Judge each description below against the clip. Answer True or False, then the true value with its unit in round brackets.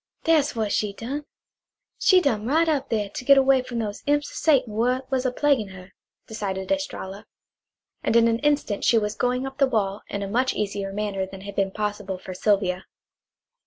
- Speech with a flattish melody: False (5.0 semitones)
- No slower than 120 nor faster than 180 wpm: False (200 wpm)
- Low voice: False (225 Hz)